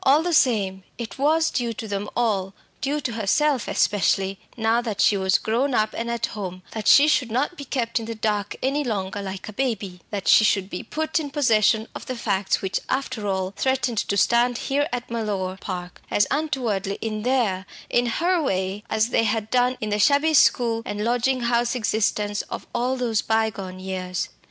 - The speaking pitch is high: Yes, high, 225 Hz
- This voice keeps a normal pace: Yes, average, 195 wpm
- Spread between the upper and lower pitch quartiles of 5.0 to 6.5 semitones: No, average, 4.0 semitones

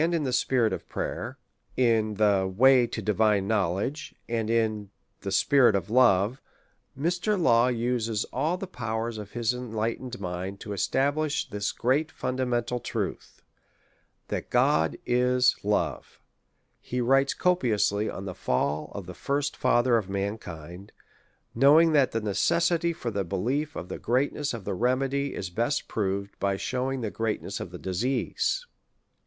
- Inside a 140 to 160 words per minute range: Yes, average, 155 wpm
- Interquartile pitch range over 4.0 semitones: Yes, average, 4.7 semitones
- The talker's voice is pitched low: Yes, low, 115 Hz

